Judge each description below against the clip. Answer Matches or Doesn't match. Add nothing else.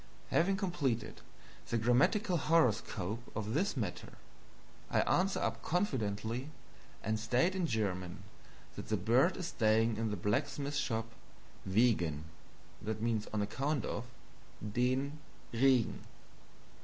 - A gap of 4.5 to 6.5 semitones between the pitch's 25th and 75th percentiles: Matches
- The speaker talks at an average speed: Doesn't match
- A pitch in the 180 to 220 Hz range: Doesn't match